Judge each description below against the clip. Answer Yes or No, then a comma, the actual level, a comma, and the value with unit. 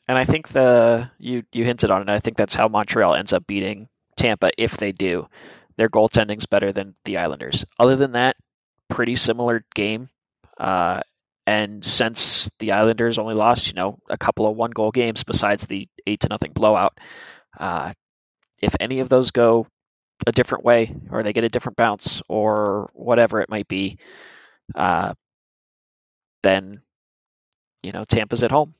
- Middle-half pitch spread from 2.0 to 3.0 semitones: Yes, average, 2.7 semitones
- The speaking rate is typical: Yes, average, 165 wpm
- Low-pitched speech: Yes, low, 115 Hz